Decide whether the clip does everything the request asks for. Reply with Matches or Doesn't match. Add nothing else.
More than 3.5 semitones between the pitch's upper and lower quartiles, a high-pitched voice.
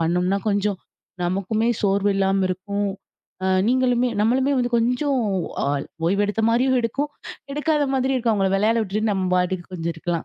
Matches